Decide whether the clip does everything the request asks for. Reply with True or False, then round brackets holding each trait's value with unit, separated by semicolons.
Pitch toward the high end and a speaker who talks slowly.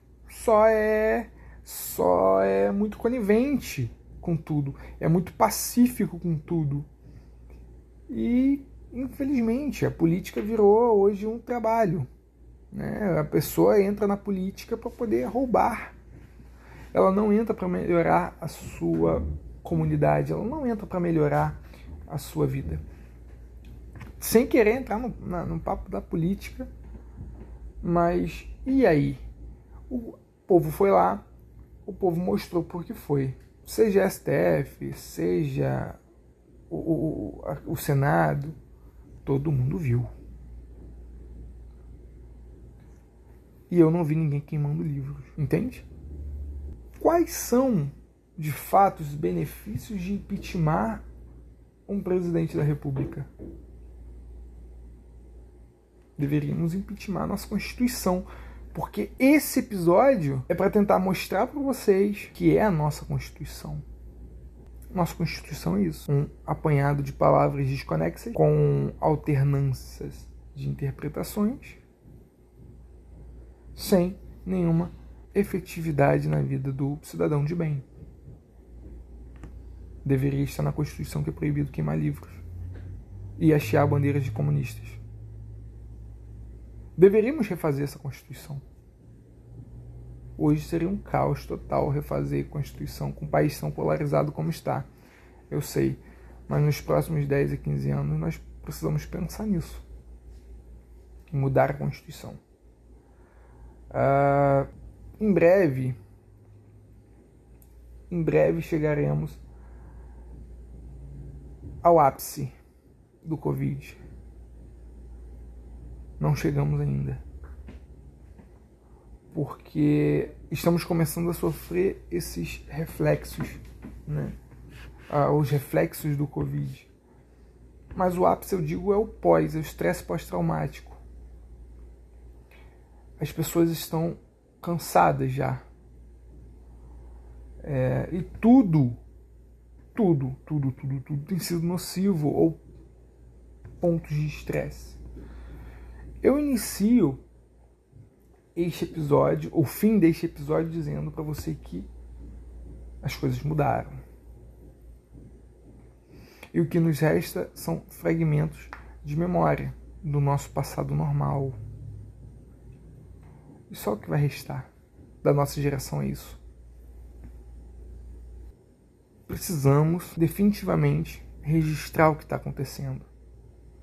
False (130 Hz; 100 wpm)